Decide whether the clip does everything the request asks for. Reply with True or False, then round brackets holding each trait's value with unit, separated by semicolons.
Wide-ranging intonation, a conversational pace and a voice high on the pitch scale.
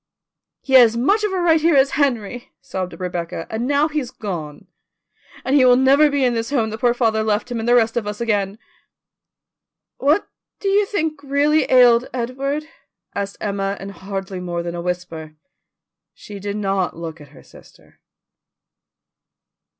True (5.9 semitones; 175 wpm; 230 Hz)